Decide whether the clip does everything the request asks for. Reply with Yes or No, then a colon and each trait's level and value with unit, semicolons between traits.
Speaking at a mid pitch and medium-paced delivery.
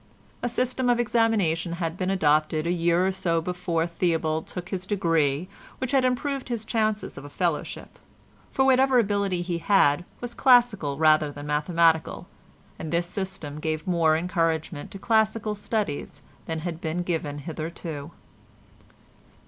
Yes: medium, 175 Hz; average, 150 wpm